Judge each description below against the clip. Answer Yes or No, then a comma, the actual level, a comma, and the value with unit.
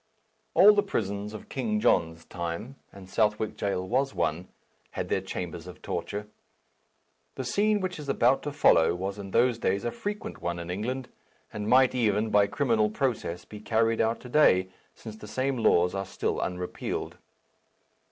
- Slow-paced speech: No, average, 170 wpm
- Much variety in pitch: Yes, wide, 5.7 semitones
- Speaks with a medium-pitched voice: No, low, 105 Hz